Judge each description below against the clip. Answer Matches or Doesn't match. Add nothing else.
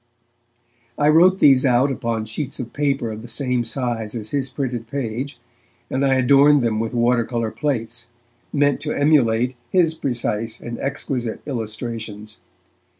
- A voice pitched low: Matches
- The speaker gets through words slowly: Doesn't match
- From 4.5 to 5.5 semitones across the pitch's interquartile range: Doesn't match